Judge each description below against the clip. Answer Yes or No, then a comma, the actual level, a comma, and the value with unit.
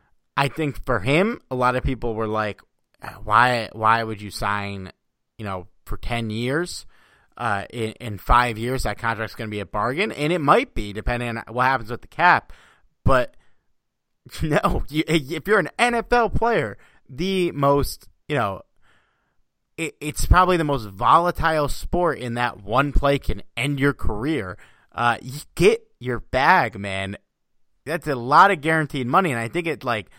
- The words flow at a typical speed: Yes, average, 175 wpm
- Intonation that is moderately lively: No, wide, 5.8 semitones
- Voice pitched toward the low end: Yes, low, 125 Hz